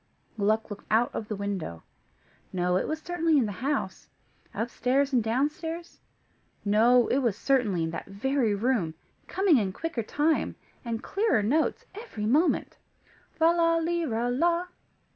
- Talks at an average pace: Yes, average, 145 wpm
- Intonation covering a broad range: Yes, wide, 7.2 semitones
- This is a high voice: Yes, very high, 250 Hz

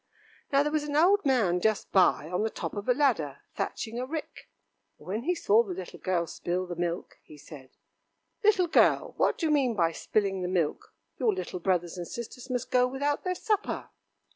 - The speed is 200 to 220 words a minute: Yes, fast, 205 wpm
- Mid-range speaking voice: No, high, 220 Hz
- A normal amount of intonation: No, wide, 8.1 semitones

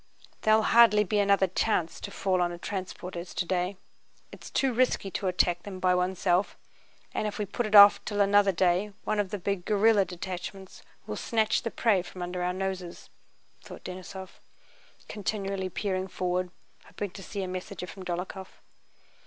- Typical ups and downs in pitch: No, narrow, 2.2 semitones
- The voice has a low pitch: No, high, 190 Hz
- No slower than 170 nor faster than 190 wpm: Yes, average, 175 wpm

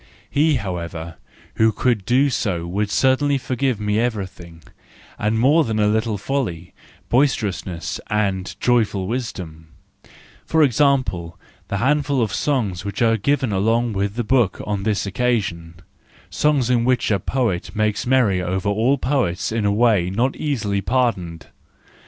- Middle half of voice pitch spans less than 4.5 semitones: No, average, 4.9 semitones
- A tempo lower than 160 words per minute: Yes, average, 140 wpm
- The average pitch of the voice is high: No, low, 110 Hz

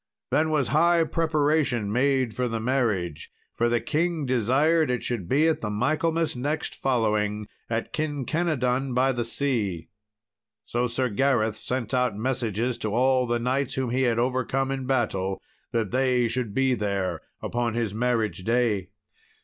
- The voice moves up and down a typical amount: Yes, average, 3.1 semitones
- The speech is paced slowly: No, average, 155 wpm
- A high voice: No, low, 125 Hz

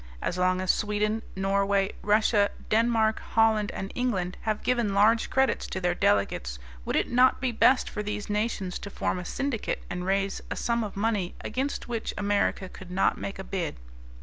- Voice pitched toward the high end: Yes, high, 205 Hz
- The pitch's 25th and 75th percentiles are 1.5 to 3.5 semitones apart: Yes, average, 2.8 semitones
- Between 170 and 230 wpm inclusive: Yes, average, 180 wpm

